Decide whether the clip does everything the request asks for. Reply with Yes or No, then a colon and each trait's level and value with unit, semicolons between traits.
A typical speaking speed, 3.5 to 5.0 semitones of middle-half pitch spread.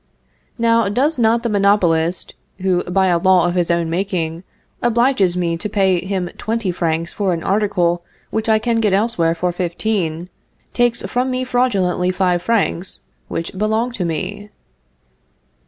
Yes: average, 155 wpm; average, 4.2 semitones